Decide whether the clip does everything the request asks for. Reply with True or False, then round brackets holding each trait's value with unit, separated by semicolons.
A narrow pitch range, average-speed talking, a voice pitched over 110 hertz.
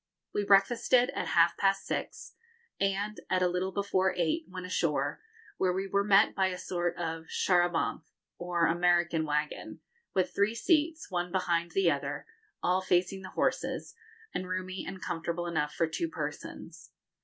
True (2.2 semitones; 165 wpm; 185 Hz)